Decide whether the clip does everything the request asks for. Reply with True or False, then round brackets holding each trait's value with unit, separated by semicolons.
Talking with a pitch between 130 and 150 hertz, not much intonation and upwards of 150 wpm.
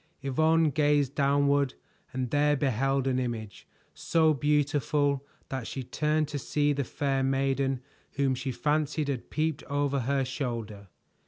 False (140 Hz; 1.9 semitones; 140 wpm)